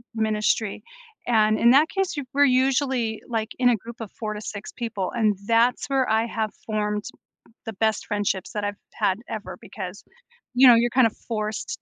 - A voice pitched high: Yes, high, 225 Hz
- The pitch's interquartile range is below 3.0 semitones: Yes, narrow, 2.5 semitones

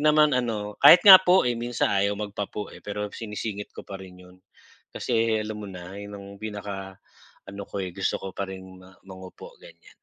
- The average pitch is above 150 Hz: No, low, 100 Hz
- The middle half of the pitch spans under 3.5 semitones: Yes, average, 2.9 semitones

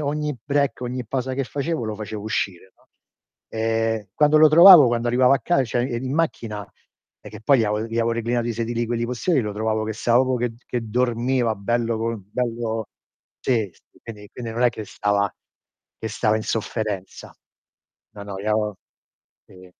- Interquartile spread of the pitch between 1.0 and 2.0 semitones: No, average, 2.7 semitones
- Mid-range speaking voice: No, low, 115 Hz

